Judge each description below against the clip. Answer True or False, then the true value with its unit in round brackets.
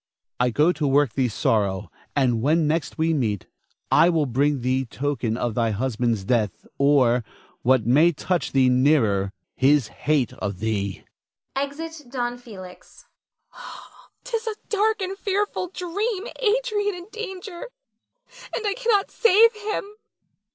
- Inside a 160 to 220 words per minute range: False (140 wpm)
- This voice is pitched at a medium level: True (150 Hz)